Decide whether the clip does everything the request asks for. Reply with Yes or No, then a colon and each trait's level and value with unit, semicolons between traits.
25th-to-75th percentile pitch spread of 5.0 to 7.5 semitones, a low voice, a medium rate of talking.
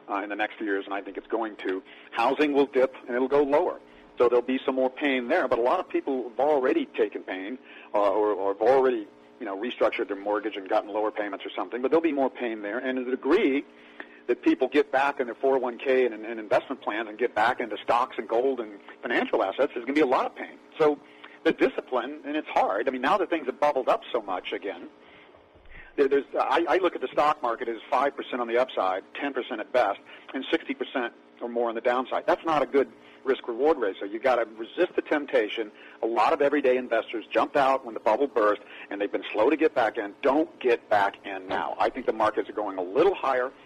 No: average, 5.3 semitones; low, 125 Hz; fast, 240 wpm